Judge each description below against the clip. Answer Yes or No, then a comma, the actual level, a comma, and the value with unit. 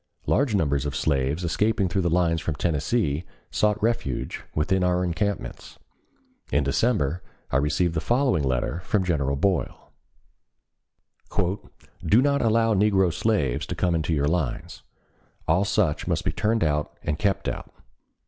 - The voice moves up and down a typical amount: No, wide, 5.9 semitones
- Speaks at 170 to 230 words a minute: No, average, 145 wpm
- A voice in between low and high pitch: No, very low, 85 Hz